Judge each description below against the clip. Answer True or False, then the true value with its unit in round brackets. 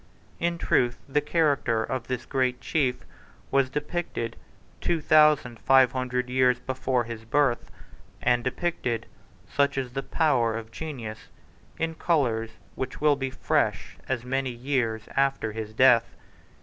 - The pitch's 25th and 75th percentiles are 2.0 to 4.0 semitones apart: True (3.3 semitones)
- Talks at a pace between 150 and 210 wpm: False (135 wpm)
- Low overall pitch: True (130 Hz)